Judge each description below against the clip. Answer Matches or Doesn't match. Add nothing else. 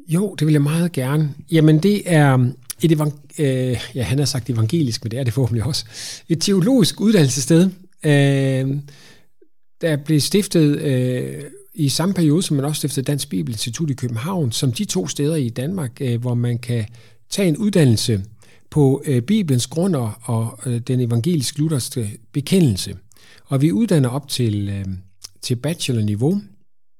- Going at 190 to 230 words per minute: Doesn't match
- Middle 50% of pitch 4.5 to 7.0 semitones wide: Matches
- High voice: Doesn't match